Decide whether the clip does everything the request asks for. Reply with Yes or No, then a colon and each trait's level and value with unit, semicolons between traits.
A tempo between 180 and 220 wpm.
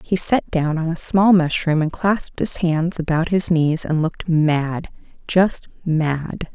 No: average, 165 wpm